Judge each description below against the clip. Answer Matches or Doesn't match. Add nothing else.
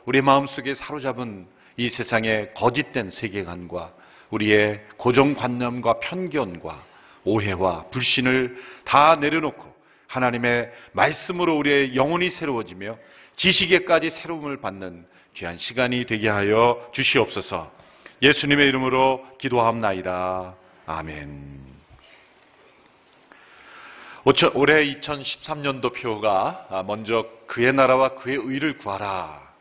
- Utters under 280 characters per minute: Matches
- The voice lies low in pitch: Matches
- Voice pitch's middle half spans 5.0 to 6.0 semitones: Matches